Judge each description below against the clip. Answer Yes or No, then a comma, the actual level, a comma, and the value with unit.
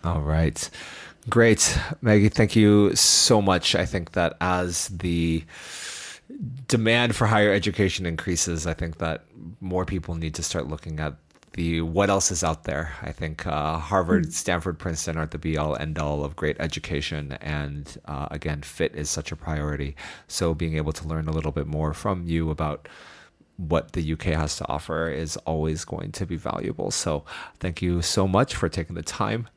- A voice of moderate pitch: No, very low, 80 Hz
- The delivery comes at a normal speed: Yes, average, 185 wpm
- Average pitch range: Yes, average, 3.3 semitones